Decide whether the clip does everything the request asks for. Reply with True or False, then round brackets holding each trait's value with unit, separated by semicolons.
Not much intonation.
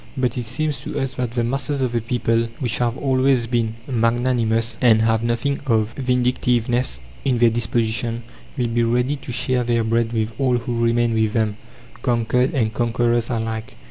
True (1.6 semitones)